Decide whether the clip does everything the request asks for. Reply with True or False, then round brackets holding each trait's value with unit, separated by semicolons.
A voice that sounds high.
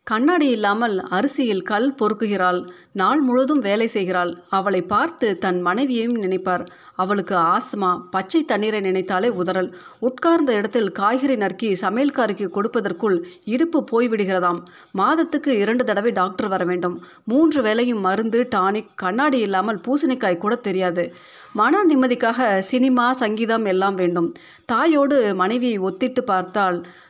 True (210 Hz)